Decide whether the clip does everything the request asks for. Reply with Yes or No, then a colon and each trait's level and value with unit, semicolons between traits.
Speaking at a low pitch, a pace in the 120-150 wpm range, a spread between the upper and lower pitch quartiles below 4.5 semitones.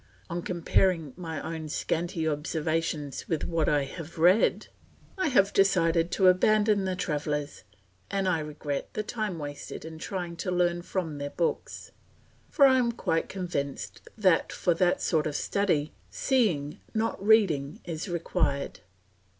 No: medium, 170 Hz; average, 145 wpm; average, 3.8 semitones